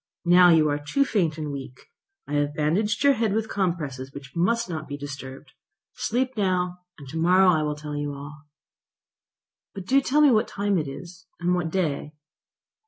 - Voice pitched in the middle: Yes, medium, 165 Hz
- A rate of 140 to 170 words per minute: No, average, 185 wpm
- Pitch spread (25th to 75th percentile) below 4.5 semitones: No, average, 5.2 semitones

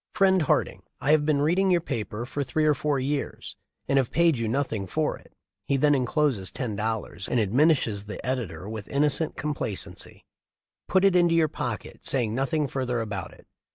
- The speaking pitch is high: No, low, 135 Hz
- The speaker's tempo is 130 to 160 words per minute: No, average, 190 wpm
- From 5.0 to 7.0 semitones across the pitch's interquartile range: Yes, average, 5.3 semitones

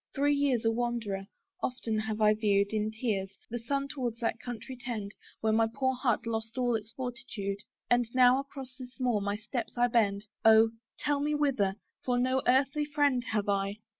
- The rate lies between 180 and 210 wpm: Yes, average, 185 wpm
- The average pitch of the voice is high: Yes, high, 235 Hz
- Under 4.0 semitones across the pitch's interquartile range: Yes, average, 3.2 semitones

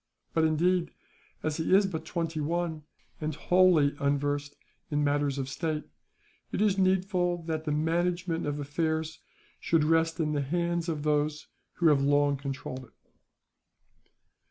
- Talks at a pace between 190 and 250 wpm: No, average, 145 wpm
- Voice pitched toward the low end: No, medium, 160 Hz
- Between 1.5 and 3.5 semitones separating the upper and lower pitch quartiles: Yes, average, 2.9 semitones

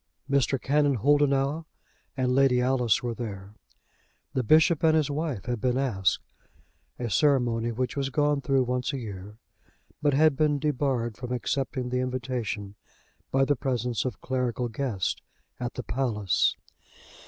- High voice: No, low, 130 Hz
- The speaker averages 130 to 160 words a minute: Yes, average, 145 wpm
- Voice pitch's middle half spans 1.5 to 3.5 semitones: Yes, average, 2.8 semitones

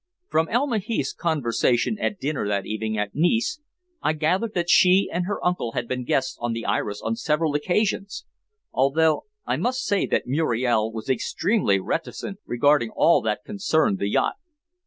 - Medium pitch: Yes, medium, 150 Hz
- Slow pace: No, average, 165 wpm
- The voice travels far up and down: Yes, wide, 8.1 semitones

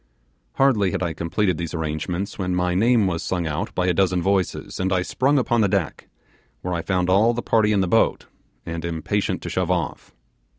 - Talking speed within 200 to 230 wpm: Yes, fast, 205 wpm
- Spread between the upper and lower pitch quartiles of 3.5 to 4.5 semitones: No, average, 3.1 semitones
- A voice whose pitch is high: No, very low, 90 Hz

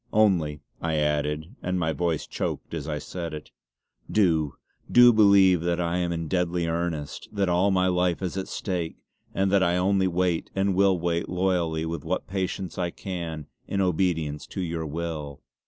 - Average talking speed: Yes, average, 180 wpm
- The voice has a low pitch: Yes, very low, 85 Hz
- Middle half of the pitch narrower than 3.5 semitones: Yes, narrow, 2.6 semitones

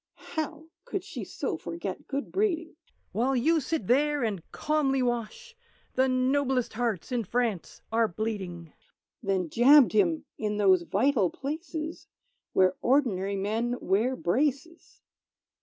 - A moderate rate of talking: No, slow, 125 wpm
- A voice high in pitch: Yes, high, 245 Hz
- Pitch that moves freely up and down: Yes, wide, 6.1 semitones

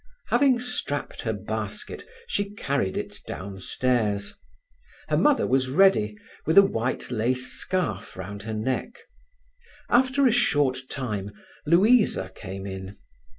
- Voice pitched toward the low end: Yes, low, 130 Hz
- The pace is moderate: No, slow, 120 wpm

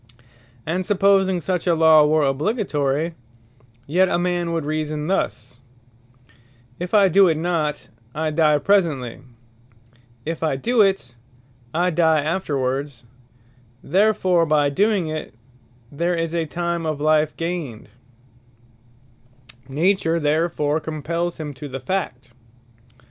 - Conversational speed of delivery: No, slow, 115 wpm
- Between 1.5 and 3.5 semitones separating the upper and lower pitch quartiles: Yes, average, 3.1 semitones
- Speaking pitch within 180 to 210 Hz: No, medium, 160 Hz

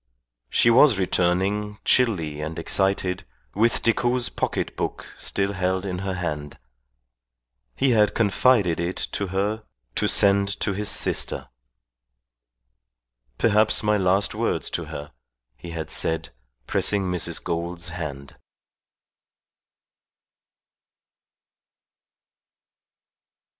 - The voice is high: No, very low, 95 Hz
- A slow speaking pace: Yes, slow, 100 wpm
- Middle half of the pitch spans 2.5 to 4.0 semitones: Yes, average, 3.3 semitones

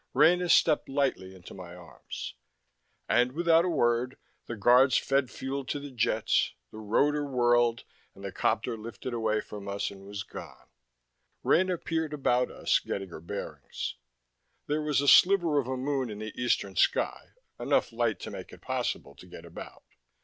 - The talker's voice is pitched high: No, low, 125 Hz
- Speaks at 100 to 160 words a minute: No, average, 170 wpm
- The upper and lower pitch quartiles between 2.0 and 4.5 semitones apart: No, average, 5.3 semitones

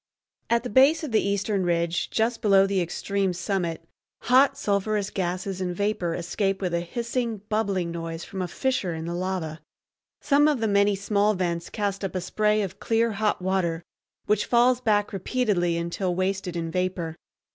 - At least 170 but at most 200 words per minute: Yes, average, 175 wpm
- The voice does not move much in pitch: No, average, 3.5 semitones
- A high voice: Yes, high, 195 Hz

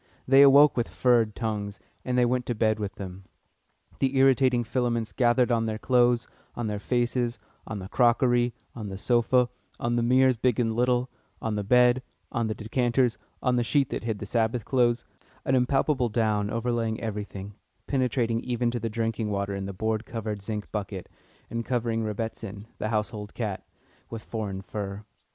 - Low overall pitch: Yes, low, 115 Hz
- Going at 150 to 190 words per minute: Yes, average, 175 wpm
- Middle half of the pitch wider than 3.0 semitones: No, narrow, 2.5 semitones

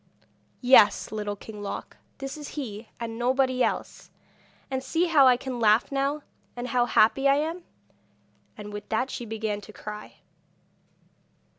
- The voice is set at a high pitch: Yes, high, 245 Hz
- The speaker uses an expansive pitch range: No, average, 4.2 semitones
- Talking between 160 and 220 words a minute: No, average, 150 wpm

